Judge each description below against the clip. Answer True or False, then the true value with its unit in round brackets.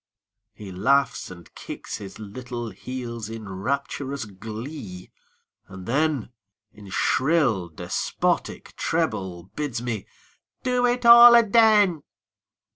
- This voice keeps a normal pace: False (105 wpm)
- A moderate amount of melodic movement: False (7.6 semitones)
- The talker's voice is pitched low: True (120 Hz)